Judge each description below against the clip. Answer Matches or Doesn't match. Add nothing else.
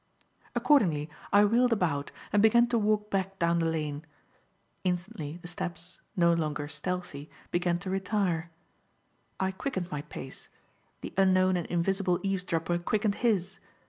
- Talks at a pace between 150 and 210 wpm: Doesn't match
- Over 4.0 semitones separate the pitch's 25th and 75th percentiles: Doesn't match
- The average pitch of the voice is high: Doesn't match